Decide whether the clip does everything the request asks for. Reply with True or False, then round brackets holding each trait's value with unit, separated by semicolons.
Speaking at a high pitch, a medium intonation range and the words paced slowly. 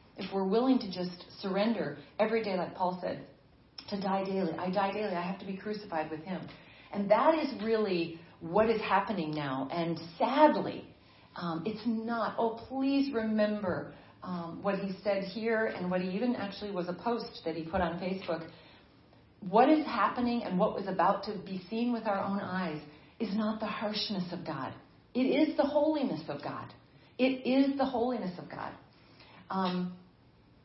False (200 Hz; 4.4 semitones; 180 wpm)